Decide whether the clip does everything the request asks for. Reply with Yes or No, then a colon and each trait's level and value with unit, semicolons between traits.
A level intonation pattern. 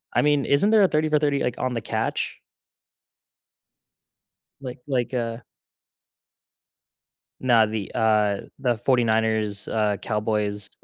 No: average, 4.1 semitones